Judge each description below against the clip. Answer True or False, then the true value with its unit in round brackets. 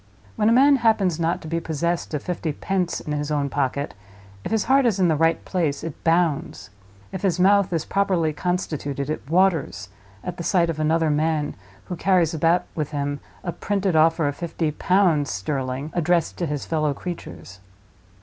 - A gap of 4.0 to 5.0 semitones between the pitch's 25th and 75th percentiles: False (3.5 semitones)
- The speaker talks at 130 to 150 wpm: False (185 wpm)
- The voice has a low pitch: False (165 Hz)